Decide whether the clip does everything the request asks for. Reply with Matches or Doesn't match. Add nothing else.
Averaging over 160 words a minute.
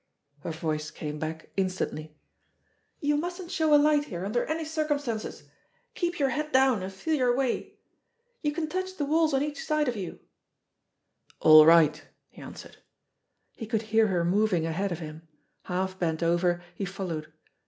Matches